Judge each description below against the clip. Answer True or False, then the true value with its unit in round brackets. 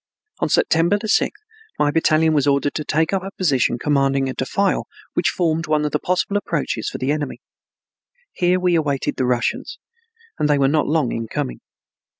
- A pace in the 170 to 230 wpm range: True (180 wpm)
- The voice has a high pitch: False (150 Hz)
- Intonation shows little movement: False (3.4 semitones)